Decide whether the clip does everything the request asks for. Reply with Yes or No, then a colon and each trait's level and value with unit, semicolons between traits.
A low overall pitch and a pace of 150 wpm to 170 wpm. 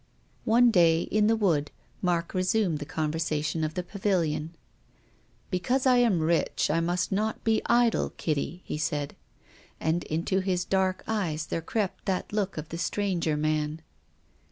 No: medium, 175 Hz; average, 155 wpm